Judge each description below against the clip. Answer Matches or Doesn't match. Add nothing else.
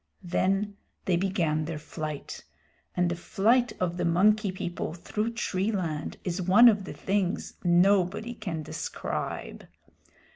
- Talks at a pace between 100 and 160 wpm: Matches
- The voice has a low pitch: Doesn't match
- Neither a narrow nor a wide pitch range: Matches